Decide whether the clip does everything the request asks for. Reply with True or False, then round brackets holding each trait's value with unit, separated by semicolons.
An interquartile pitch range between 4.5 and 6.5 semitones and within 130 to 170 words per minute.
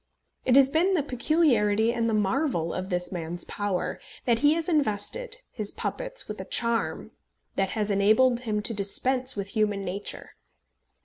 True (5.1 semitones; 165 wpm)